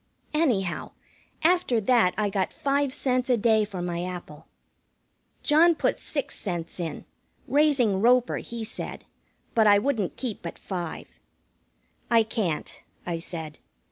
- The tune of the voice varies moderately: No, wide, 6.0 semitones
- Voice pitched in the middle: No, high, 220 Hz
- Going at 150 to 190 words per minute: No, slow, 135 wpm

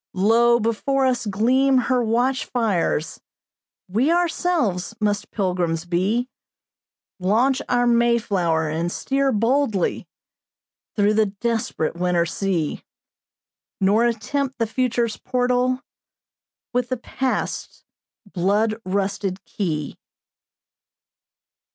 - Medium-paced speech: No, slow, 95 wpm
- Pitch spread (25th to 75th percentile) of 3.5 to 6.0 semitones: Yes, average, 4.6 semitones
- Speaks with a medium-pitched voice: No, high, 225 Hz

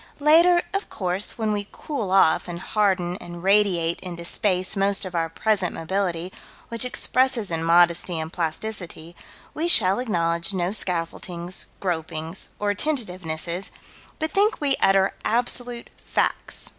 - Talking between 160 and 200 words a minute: No, slow, 135 wpm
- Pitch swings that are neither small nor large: Yes, average, 4.3 semitones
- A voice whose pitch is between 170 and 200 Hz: Yes, high, 190 Hz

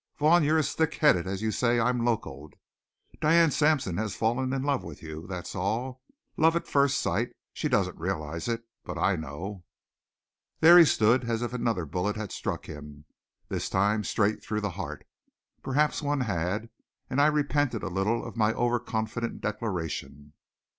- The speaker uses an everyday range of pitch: No, wide, 5.9 semitones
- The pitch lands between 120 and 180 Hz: No, low, 110 Hz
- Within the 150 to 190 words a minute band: Yes, average, 165 wpm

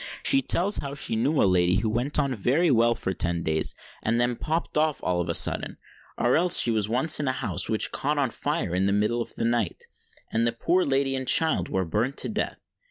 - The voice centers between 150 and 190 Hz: No, low, 120 Hz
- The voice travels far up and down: Yes, wide, 5.8 semitones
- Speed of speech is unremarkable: No, fast, 235 wpm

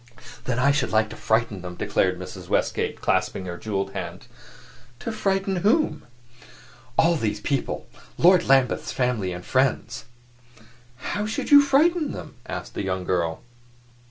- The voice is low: Yes, low, 125 Hz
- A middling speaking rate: Yes, average, 145 wpm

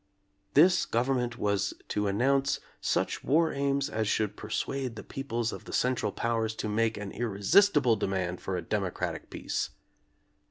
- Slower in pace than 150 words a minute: No, average, 155 wpm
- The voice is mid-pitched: No, low, 115 Hz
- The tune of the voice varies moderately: Yes, average, 4.7 semitones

